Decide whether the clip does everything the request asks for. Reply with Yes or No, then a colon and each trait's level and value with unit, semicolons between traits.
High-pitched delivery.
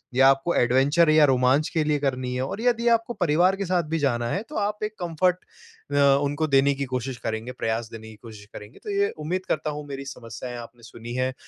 No: medium, 140 Hz